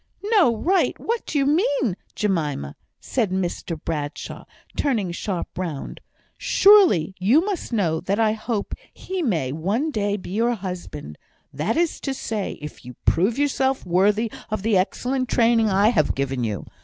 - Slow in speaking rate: No, average, 155 wpm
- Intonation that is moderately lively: No, wide, 7.3 semitones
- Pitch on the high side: Yes, high, 210 Hz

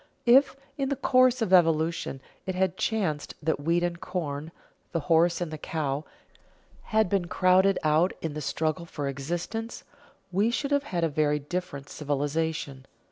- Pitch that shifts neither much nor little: Yes, average, 3.9 semitones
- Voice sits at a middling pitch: Yes, medium, 170 Hz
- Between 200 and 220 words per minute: No, average, 160 wpm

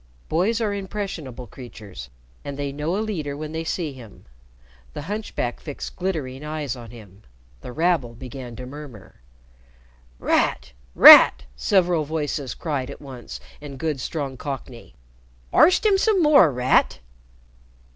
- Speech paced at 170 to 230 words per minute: No, slow, 135 wpm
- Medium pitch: Yes, medium, 145 Hz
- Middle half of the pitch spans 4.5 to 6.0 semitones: Yes, wide, 5.4 semitones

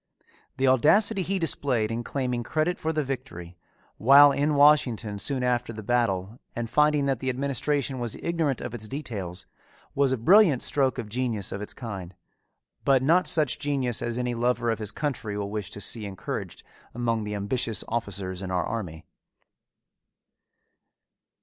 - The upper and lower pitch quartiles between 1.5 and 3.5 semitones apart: No, average, 4.8 semitones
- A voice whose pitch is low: Yes, low, 120 Hz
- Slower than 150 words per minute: No, average, 160 wpm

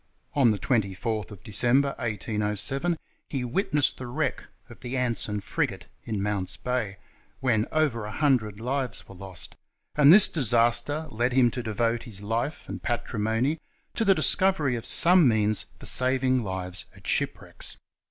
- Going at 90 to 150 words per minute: Yes, average, 145 wpm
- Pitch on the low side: Yes, low, 120 Hz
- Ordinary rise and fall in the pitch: Yes, average, 4.3 semitones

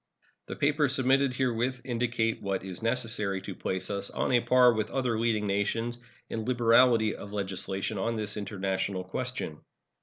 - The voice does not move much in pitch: No, average, 3.7 semitones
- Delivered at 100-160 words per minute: Yes, average, 155 wpm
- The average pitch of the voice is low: Yes, low, 115 Hz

